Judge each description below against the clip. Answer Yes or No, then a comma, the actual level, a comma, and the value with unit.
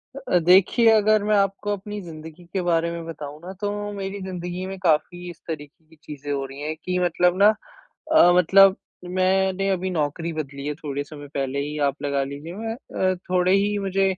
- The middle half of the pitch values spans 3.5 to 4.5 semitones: Yes, average, 4.1 semitones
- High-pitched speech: No, medium, 180 Hz